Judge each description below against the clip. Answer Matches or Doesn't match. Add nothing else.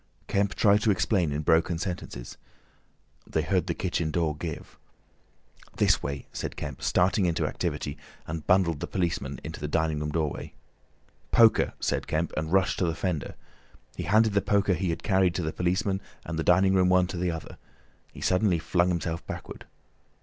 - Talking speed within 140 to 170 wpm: Doesn't match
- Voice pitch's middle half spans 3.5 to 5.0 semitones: Doesn't match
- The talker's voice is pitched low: Matches